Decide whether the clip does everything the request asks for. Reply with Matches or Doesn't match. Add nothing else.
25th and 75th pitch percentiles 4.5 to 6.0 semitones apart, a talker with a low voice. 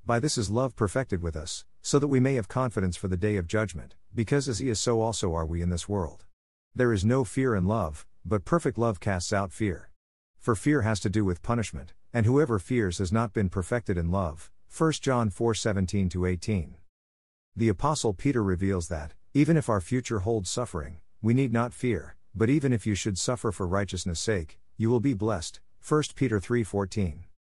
Matches